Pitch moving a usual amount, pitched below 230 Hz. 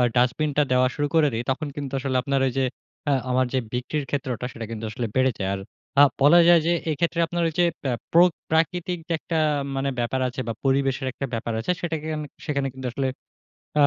Yes: average, 3.6 semitones; medium, 140 Hz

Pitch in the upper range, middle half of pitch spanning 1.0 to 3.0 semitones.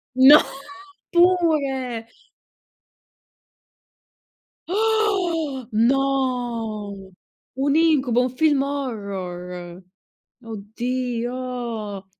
No: very high, 255 Hz; average, 4.6 semitones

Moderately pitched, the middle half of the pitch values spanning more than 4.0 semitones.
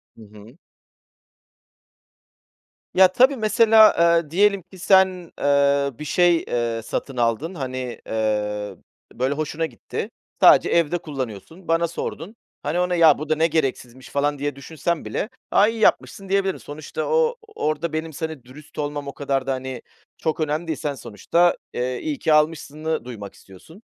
Yes: medium, 155 Hz; average, 5.0 semitones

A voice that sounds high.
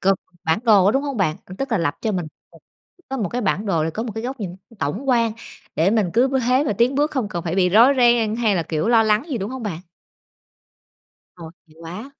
Yes: high, 215 Hz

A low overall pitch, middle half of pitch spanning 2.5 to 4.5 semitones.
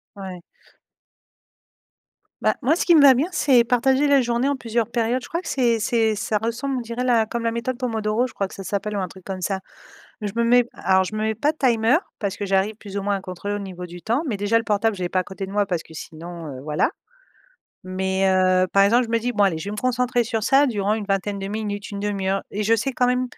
No: high, 215 Hz; average, 3.8 semitones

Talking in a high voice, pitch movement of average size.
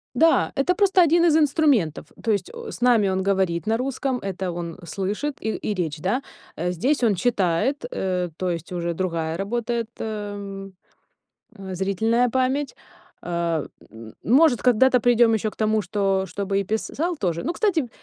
No: high, 210 Hz; wide, 5.7 semitones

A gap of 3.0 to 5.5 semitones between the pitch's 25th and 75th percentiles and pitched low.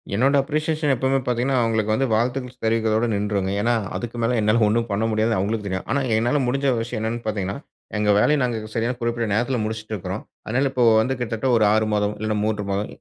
No: narrow, 2.6 semitones; low, 115 Hz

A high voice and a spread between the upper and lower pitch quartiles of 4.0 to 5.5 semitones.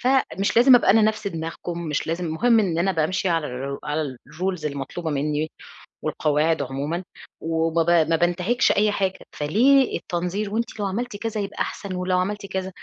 No: medium, 180 Hz; average, 4.4 semitones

